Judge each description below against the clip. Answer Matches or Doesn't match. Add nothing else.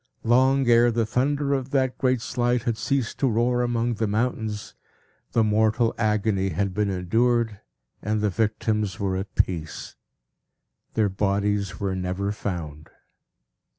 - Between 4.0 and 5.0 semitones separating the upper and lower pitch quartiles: Doesn't match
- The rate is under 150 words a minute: Matches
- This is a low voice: Matches